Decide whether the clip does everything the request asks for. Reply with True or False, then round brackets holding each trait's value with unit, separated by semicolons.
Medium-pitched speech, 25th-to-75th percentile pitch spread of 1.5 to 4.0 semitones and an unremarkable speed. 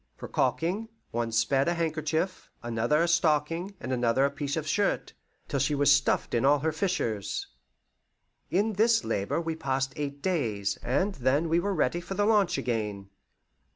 False (150 Hz; 5.1 semitones; 165 wpm)